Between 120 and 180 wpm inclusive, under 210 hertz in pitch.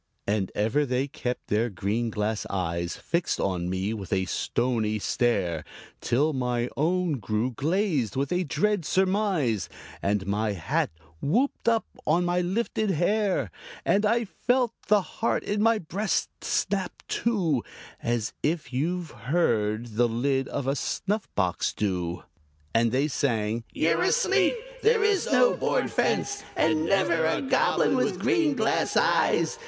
Yes: average, 145 wpm; medium, 140 Hz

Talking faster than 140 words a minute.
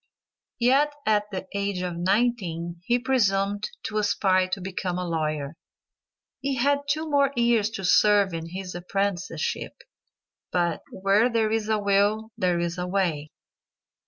No: slow, 135 wpm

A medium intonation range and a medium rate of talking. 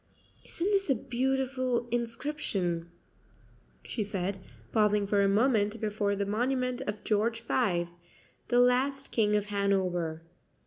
No: average, 4.0 semitones; slow, 125 wpm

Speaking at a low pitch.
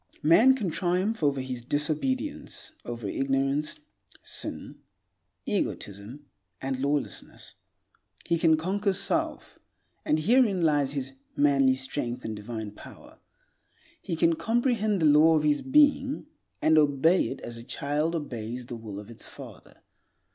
No: medium, 150 Hz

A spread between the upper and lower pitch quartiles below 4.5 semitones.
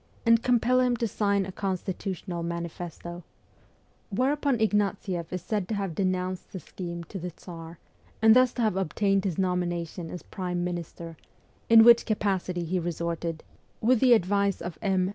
Yes: average, 3.8 semitones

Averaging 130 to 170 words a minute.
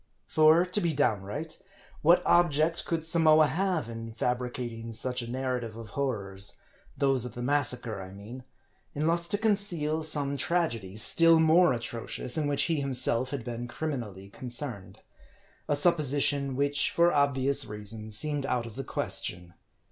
Yes: average, 155 wpm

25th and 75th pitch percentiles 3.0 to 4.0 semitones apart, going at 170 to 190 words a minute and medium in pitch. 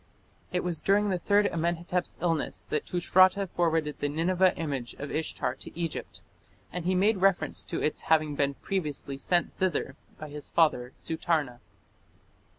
No: average, 3.4 semitones; average, 155 wpm; medium, 165 Hz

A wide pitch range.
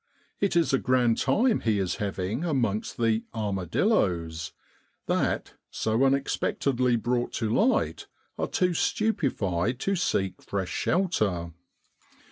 Yes: wide, 7.0 semitones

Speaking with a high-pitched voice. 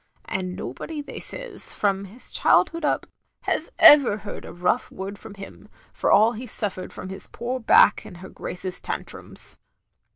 Yes: high, 205 Hz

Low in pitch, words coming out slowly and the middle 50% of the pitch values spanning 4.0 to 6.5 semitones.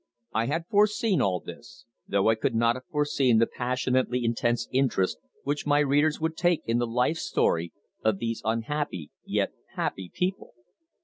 No: low, 125 Hz; average, 165 wpm; average, 4.5 semitones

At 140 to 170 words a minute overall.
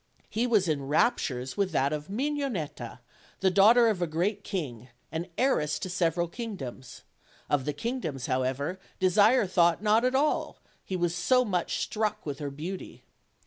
Yes: average, 165 wpm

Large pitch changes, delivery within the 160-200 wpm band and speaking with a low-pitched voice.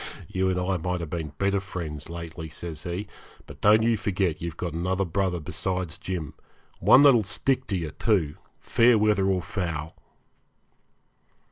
No: average, 3.1 semitones; average, 165 wpm; very low, 90 Hz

